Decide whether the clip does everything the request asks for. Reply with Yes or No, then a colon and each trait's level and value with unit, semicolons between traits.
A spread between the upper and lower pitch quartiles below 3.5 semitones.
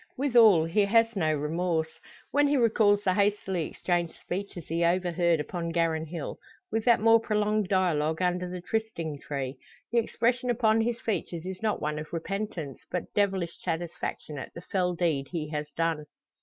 No: average, 4.7 semitones